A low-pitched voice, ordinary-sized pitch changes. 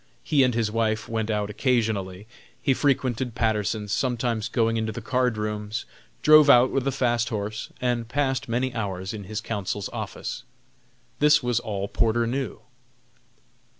Yes: low, 115 Hz; average, 3.0 semitones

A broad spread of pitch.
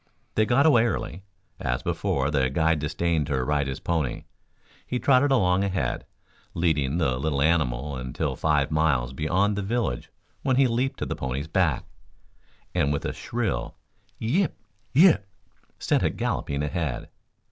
Yes: wide, 7.1 semitones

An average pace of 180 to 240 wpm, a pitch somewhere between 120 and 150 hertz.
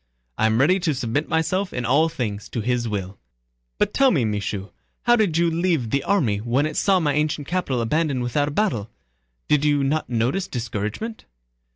Yes: average, 190 wpm; medium, 140 Hz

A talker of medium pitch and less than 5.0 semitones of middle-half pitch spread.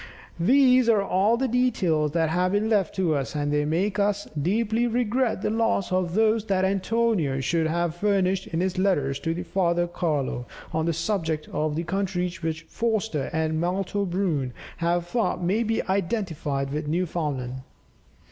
Yes: medium, 180 Hz; average, 4.5 semitones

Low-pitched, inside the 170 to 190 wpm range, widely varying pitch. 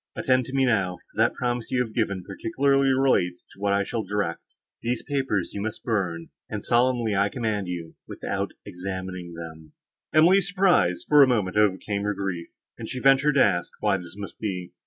Yes: low, 105 Hz; average, 185 wpm; wide, 5.7 semitones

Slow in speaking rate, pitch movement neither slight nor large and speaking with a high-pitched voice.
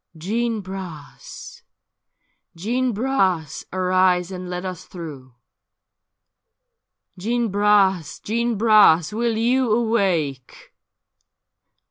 Yes: slow, 90 wpm; average, 4.3 semitones; high, 195 Hz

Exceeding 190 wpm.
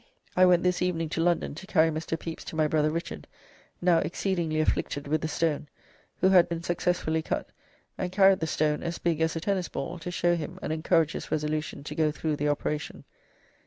Yes: fast, 205 wpm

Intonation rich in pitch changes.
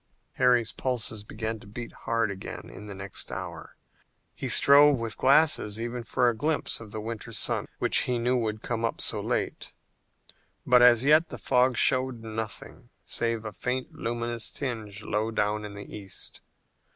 No: narrow, 2.5 semitones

